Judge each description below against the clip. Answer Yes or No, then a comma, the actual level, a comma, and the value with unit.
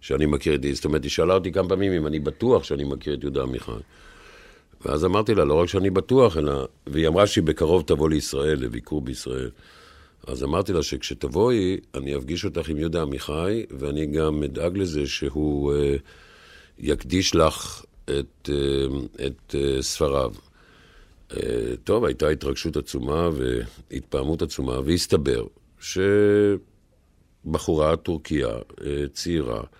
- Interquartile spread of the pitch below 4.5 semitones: Yes, average, 3.8 semitones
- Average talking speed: Yes, average, 140 wpm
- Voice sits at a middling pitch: No, very low, 75 Hz